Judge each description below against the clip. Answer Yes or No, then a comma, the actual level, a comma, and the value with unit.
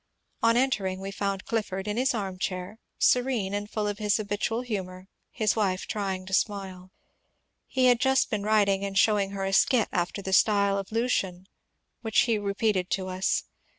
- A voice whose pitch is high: Yes, high, 200 Hz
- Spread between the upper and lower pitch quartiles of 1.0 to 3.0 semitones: Yes, narrow, 2.6 semitones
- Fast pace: No, average, 180 wpm